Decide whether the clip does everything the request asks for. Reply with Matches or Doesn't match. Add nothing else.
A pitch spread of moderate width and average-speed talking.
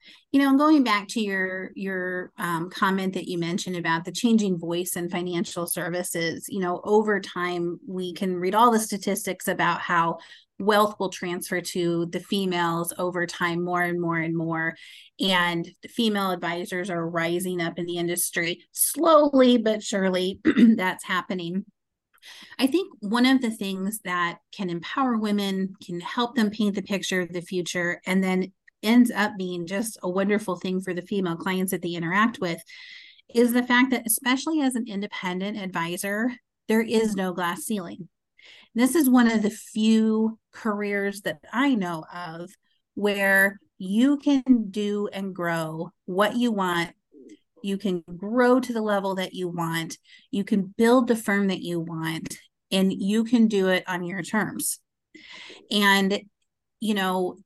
Matches